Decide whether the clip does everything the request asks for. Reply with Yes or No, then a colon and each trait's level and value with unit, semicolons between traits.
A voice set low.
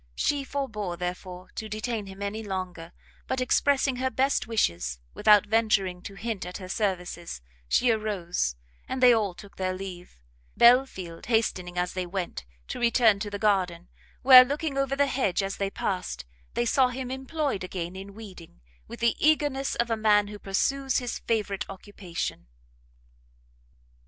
No: high, 210 Hz